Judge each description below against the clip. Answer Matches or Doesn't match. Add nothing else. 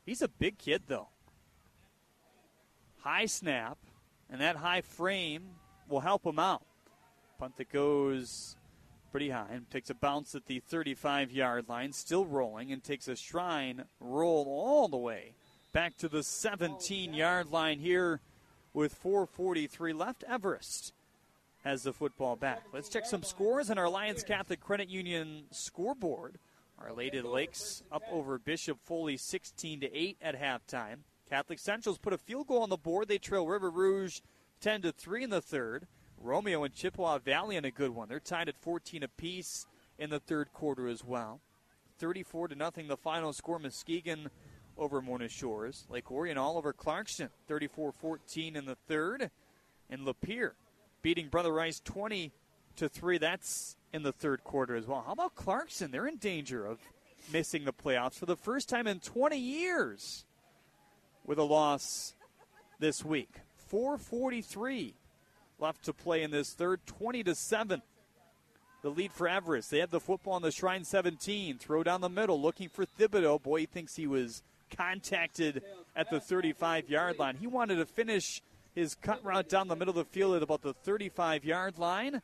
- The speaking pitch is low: Doesn't match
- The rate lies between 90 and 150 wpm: Doesn't match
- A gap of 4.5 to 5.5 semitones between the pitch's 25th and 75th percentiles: Matches